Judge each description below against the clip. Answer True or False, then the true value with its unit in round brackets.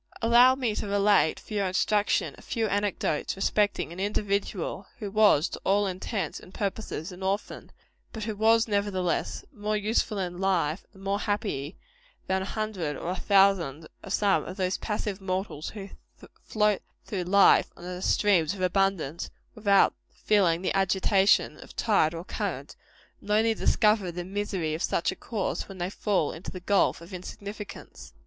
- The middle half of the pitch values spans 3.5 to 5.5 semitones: False (2.4 semitones)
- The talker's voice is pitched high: True (195 Hz)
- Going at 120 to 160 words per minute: False (170 wpm)